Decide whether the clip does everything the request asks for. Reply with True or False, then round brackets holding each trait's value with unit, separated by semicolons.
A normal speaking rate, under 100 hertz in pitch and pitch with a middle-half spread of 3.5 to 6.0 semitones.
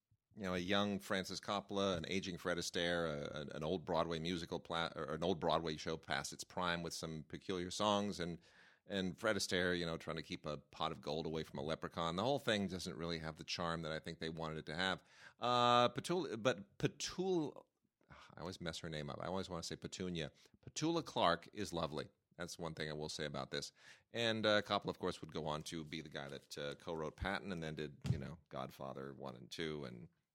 False (230 wpm; 85 Hz; 3.8 semitones)